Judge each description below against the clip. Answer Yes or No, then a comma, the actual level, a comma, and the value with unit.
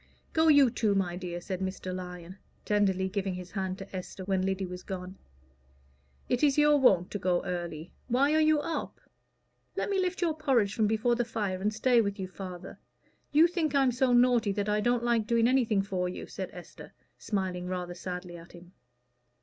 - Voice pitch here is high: Yes, high, 200 Hz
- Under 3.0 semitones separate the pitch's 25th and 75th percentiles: No, average, 5.1 semitones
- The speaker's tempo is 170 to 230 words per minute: Yes, average, 195 wpm